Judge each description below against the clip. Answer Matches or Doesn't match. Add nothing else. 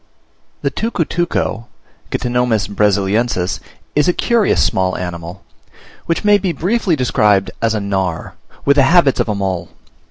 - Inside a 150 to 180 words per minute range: Doesn't match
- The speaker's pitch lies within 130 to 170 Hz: Doesn't match